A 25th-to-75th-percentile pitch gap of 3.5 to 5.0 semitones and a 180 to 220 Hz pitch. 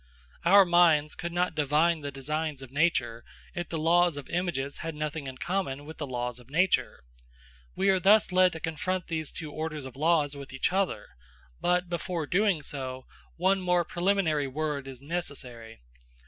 No: average, 3.9 semitones; medium, 160 Hz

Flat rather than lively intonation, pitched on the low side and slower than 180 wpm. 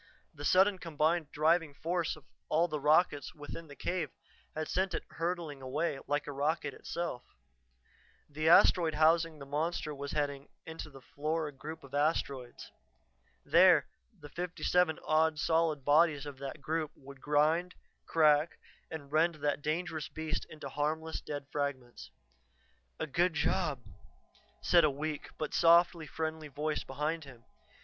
No: narrow, 2.2 semitones; medium, 155 Hz; average, 145 wpm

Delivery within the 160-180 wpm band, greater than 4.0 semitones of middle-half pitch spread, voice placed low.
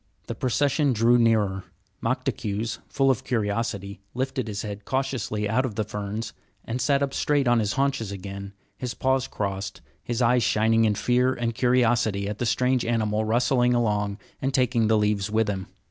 No: average, 175 wpm; average, 3.4 semitones; low, 115 Hz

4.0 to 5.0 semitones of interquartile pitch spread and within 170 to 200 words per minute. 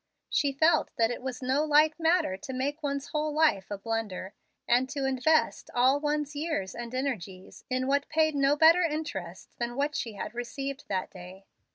Yes: average, 4.7 semitones; average, 180 wpm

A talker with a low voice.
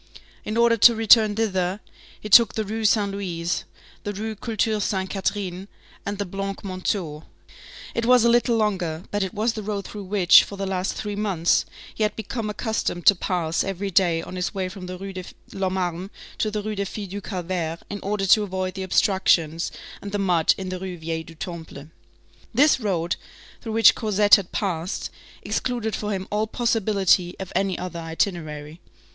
No: high, 195 Hz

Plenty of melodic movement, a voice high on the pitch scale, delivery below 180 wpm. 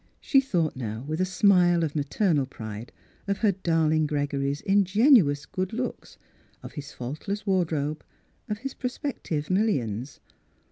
No: wide, 5.9 semitones; medium, 165 Hz; average, 150 wpm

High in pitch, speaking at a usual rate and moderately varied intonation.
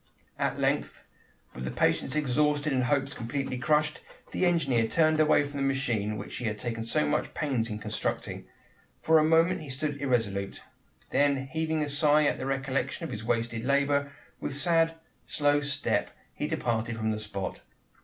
No: medium, 140 Hz; average, 170 wpm; average, 4.4 semitones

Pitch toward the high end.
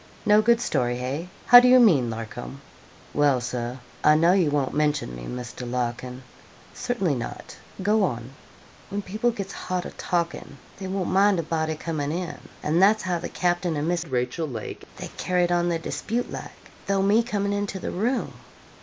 No: medium, 170 Hz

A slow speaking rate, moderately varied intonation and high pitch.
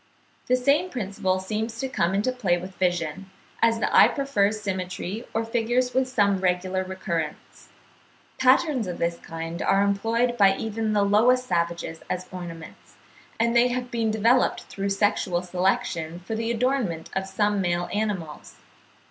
No: average, 155 wpm; average, 4.5 semitones; high, 200 Hz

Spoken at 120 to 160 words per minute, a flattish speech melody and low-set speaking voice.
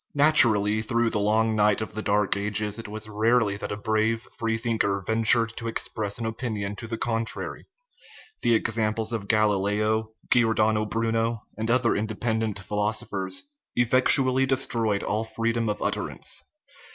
Yes: average, 155 wpm; narrow, 1.6 semitones; low, 110 Hz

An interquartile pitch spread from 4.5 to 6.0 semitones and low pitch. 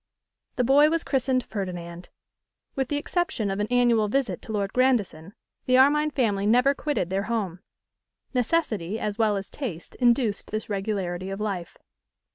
No: average, 5.0 semitones; high, 220 Hz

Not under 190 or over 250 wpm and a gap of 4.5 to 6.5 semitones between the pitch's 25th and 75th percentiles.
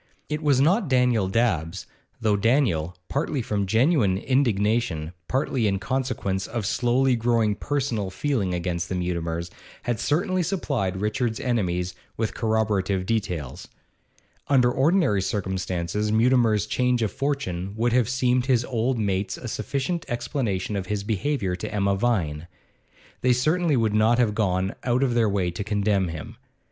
No: average, 150 wpm; average, 4.9 semitones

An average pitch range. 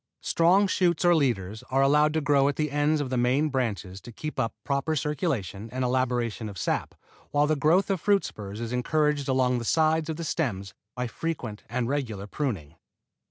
Yes: average, 4.7 semitones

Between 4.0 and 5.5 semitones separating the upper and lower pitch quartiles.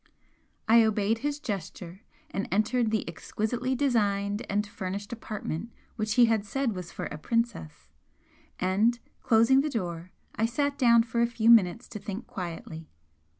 No: average, 3.2 semitones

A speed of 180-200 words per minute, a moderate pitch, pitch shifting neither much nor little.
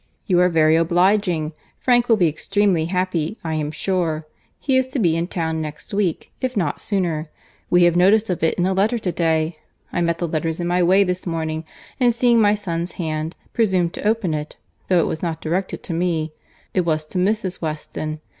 Yes: average, 195 wpm; medium, 175 Hz; average, 3.4 semitones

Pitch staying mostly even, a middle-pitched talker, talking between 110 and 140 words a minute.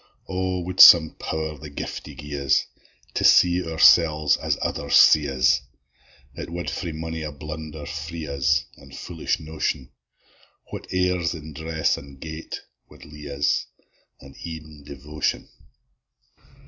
No: narrow, 2.1 semitones; very low, 75 Hz; slow, 135 wpm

